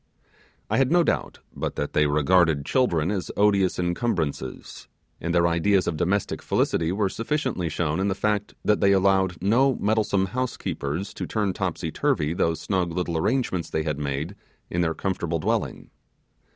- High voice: No, very low, 90 Hz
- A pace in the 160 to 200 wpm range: Yes, average, 165 wpm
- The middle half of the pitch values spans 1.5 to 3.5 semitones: No, average, 4.1 semitones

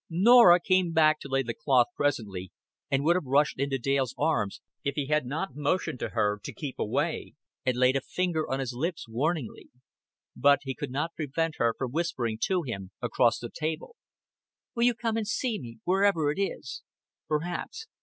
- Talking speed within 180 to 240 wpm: Yes, average, 185 wpm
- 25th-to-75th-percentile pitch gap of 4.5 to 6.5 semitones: Yes, average, 5.1 semitones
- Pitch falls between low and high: Yes, medium, 145 Hz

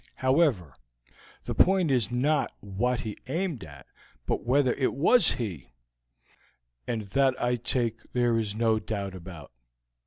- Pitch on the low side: Yes, low, 120 Hz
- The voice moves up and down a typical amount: Yes, average, 4.9 semitones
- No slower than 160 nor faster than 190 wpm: No, slow, 135 wpm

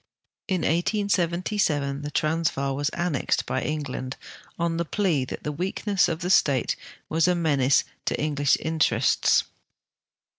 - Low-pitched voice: No, medium, 160 Hz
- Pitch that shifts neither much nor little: Yes, average, 3.7 semitones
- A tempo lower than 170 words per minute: Yes, average, 140 wpm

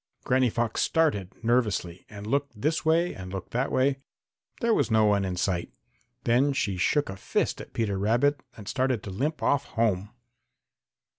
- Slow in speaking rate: No, average, 170 wpm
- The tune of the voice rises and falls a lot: Yes, wide, 5.9 semitones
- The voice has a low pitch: Yes, low, 115 Hz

